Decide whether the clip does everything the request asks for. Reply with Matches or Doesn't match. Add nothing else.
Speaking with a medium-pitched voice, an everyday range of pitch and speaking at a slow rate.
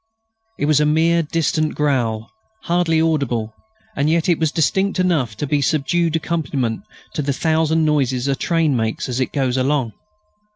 Doesn't match